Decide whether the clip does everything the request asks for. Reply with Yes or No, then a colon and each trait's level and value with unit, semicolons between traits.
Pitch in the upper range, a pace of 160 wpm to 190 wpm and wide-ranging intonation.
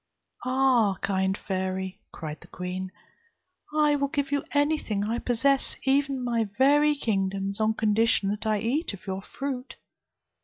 No: high, 225 Hz; average, 145 wpm; wide, 5.9 semitones